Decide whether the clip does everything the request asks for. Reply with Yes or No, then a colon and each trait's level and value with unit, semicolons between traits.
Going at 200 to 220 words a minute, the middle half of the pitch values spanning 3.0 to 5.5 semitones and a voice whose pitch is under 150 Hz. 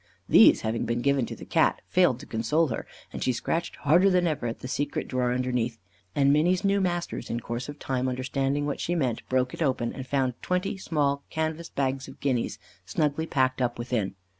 Yes: fast, 205 wpm; average, 4.2 semitones; low, 135 Hz